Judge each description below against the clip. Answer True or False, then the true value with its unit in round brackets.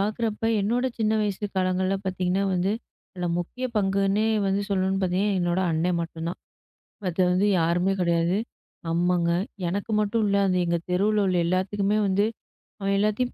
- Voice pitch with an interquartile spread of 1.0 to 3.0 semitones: True (2.4 semitones)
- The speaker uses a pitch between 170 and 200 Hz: True (190 Hz)